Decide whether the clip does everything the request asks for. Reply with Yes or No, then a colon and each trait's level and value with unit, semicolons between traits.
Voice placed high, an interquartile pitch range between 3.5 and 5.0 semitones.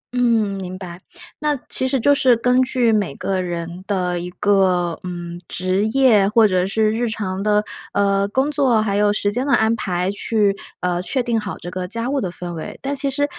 Yes: high, 205 Hz; average, 4.6 semitones